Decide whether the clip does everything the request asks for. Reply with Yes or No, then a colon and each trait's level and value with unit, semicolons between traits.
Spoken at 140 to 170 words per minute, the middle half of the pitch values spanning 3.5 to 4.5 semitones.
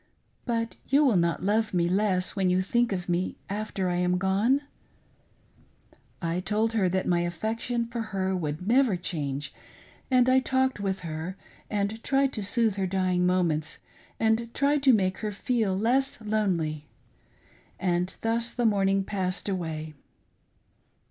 Yes: average, 155 wpm; average, 4.1 semitones